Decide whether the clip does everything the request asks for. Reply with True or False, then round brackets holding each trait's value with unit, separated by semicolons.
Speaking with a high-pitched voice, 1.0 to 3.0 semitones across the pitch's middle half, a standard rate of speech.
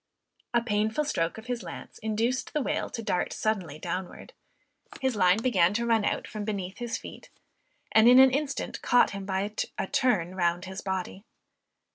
False (210 Hz; 4.1 semitones; 175 wpm)